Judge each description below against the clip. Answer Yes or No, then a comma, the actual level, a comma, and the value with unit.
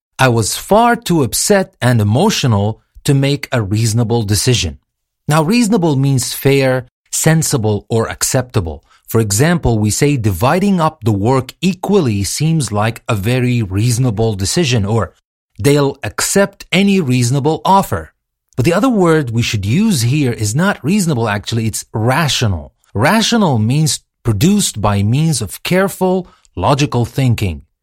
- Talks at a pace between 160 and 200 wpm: No, slow, 135 wpm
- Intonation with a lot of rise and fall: Yes, wide, 6.2 semitones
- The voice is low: Yes, low, 130 Hz